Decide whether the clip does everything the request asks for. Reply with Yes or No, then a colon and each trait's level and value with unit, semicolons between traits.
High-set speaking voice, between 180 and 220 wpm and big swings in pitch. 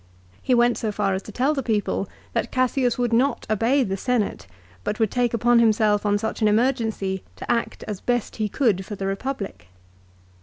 No: high, 225 Hz; average, 195 wpm; average, 3.1 semitones